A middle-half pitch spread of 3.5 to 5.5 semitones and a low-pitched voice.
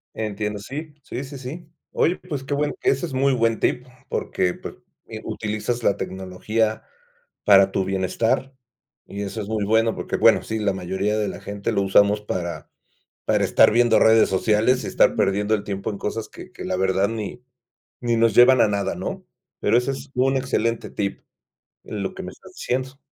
Yes: average, 3.9 semitones; low, 110 Hz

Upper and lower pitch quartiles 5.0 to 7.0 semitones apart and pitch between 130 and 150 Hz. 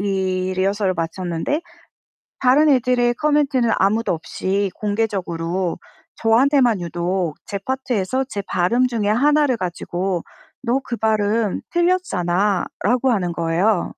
No: average, 5.3 semitones; high, 205 Hz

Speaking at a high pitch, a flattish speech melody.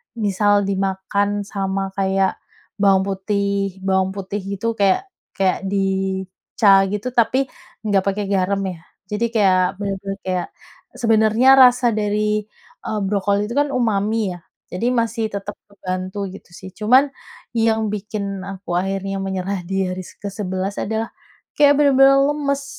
Yes: high, 200 Hz; narrow, 2.3 semitones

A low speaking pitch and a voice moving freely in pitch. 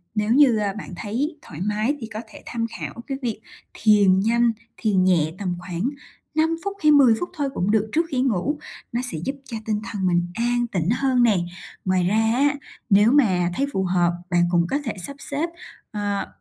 No: high, 220 Hz; wide, 5.8 semitones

